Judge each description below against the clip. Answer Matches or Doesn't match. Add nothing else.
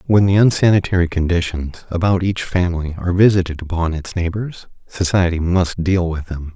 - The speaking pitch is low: Matches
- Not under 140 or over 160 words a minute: Matches